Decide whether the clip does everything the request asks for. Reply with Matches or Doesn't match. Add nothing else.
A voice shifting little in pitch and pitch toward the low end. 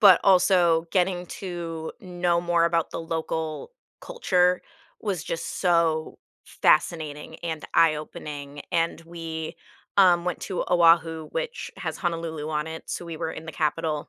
Doesn't match